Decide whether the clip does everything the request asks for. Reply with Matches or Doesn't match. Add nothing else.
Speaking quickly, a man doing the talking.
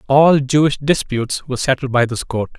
Doesn't match